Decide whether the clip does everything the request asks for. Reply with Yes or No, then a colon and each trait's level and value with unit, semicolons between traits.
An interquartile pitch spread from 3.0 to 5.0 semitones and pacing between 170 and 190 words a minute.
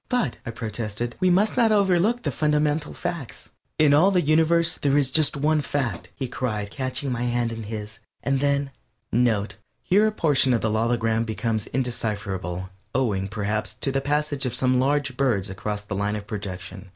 No: wide, 5.5 semitones; average, 180 wpm